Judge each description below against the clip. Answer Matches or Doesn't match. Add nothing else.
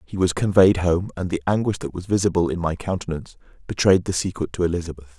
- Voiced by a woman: Doesn't match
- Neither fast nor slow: Doesn't match